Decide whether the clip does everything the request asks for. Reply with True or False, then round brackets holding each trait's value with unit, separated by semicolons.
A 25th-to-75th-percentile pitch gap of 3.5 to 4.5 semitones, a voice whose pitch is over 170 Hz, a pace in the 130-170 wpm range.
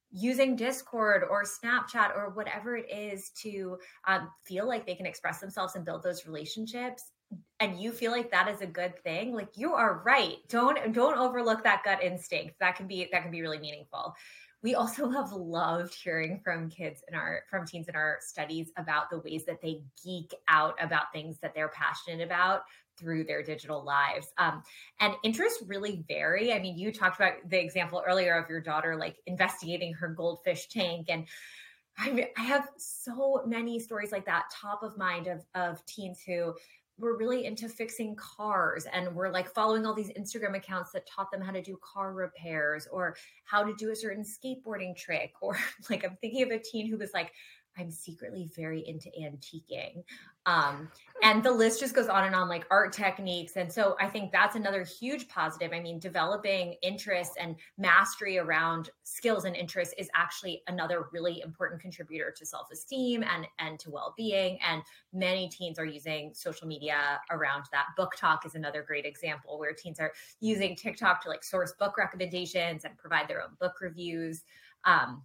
False (4.0 semitones; 185 Hz; 190 wpm)